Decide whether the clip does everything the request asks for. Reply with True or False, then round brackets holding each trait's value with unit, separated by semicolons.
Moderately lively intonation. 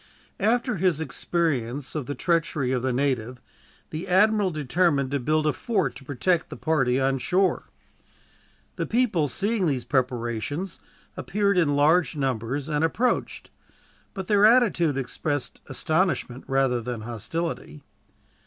False (5.8 semitones)